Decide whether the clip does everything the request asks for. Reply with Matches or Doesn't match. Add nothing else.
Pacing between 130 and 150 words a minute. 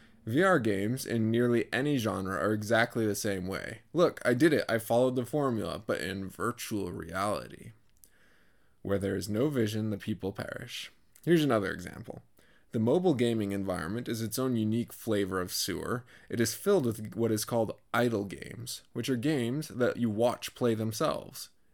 Doesn't match